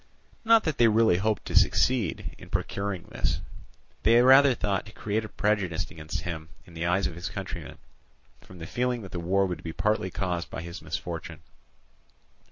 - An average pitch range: Yes, average, 4.3 semitones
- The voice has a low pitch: Yes, very low, 95 Hz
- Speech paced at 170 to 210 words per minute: Yes, average, 180 wpm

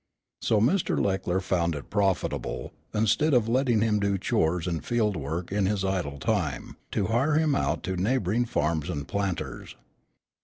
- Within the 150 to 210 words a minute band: Yes, average, 160 wpm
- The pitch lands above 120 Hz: No, low, 100 Hz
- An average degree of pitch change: Yes, average, 4.3 semitones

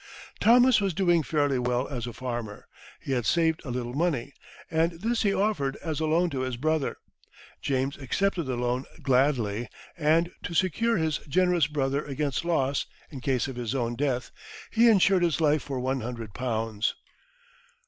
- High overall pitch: No, medium, 140 Hz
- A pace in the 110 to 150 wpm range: No, average, 170 wpm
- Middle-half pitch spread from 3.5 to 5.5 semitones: Yes, average, 5.2 semitones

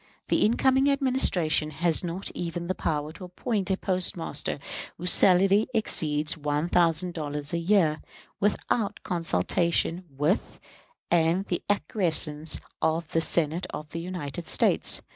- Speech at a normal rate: No, slow, 130 wpm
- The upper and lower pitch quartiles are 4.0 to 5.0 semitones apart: No, average, 3.3 semitones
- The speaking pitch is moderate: Yes, medium, 170 Hz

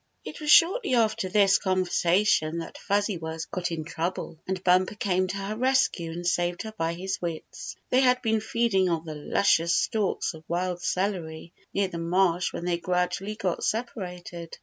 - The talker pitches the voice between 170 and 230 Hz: Yes, medium, 185 Hz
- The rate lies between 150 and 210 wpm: Yes, average, 175 wpm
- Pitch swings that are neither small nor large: Yes, average, 3.6 semitones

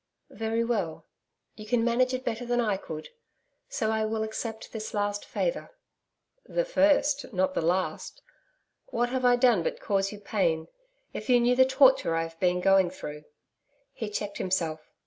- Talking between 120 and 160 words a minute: No, average, 170 wpm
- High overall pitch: Yes, high, 220 Hz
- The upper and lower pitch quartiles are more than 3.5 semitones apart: Yes, average, 4.6 semitones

